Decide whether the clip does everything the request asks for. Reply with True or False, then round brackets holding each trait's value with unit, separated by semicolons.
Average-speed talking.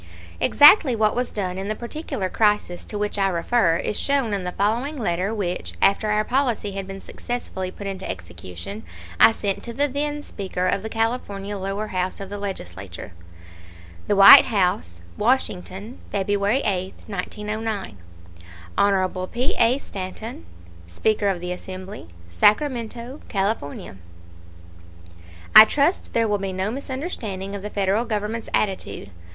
True (145 wpm)